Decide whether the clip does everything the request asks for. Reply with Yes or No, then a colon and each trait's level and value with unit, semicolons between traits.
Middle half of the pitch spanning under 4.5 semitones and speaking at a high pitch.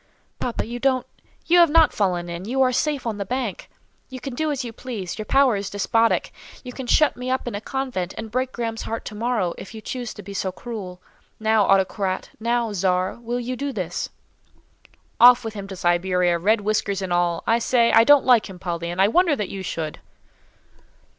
No: average, 4.8 semitones; high, 220 Hz